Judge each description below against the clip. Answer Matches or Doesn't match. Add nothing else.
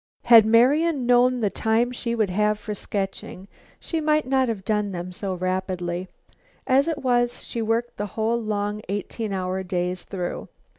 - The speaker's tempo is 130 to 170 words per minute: Matches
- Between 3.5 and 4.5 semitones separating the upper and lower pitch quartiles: Matches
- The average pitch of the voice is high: Matches